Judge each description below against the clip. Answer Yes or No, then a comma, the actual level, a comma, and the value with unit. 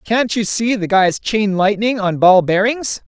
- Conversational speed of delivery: Yes, average, 190 wpm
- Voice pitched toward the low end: No, high, 210 Hz